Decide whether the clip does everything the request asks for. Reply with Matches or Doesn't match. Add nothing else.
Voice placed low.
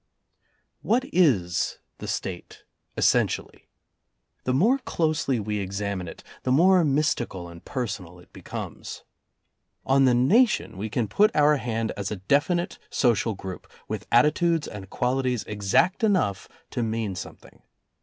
Matches